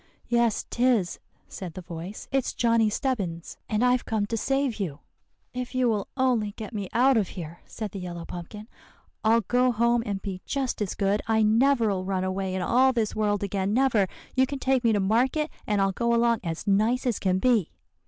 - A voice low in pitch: No, high, 220 Hz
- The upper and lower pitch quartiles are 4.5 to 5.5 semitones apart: No, average, 4.0 semitones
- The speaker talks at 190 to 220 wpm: Yes, average, 200 wpm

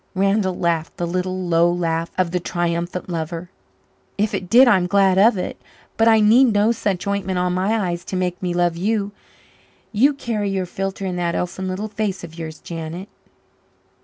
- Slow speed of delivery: No, average, 185 wpm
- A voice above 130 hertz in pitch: Yes, medium, 185 Hz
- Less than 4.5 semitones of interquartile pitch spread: Yes, average, 2.8 semitones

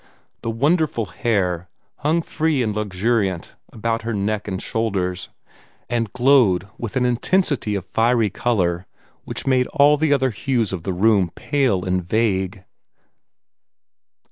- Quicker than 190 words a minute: No, slow, 135 wpm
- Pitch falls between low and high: No, low, 110 Hz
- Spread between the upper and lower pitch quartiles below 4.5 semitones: No, average, 4.9 semitones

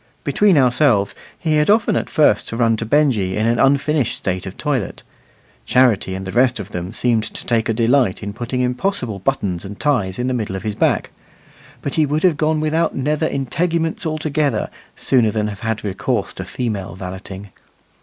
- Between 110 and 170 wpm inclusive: No, average, 190 wpm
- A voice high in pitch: No, low, 120 Hz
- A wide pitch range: Yes, wide, 6.3 semitones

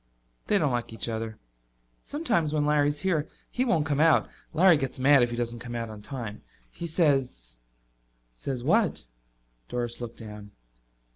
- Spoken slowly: No, average, 165 wpm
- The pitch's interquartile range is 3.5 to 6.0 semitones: Yes, wide, 5.4 semitones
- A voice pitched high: No, low, 130 Hz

